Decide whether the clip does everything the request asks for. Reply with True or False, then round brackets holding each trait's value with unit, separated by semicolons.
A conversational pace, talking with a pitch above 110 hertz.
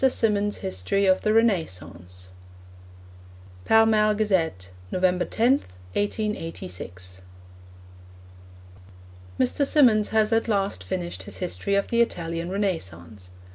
False (100 wpm; 190 Hz)